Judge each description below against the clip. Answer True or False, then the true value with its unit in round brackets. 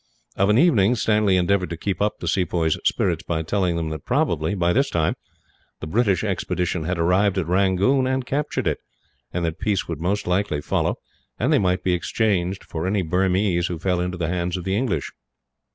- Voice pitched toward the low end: True (90 Hz)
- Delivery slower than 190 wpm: False (200 wpm)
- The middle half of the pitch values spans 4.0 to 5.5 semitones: False (3.0 semitones)